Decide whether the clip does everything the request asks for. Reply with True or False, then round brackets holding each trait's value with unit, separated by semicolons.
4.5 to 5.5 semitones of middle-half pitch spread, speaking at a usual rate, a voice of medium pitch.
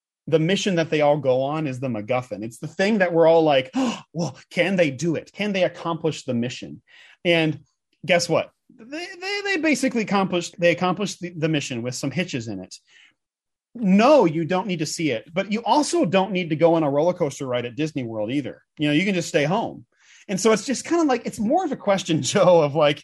False (5.1 semitones; 235 wpm; 170 Hz)